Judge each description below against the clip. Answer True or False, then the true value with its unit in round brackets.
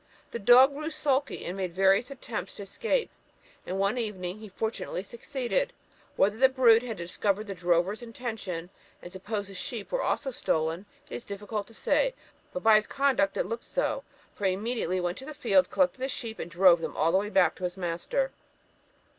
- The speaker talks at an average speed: True (190 wpm)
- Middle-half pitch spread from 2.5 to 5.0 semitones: False (5.4 semitones)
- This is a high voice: True (215 Hz)